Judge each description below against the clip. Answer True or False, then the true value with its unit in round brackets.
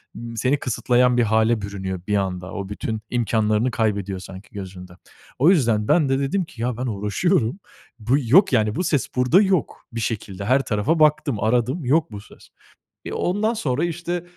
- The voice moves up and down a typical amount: False (6.1 semitones)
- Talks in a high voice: False (120 Hz)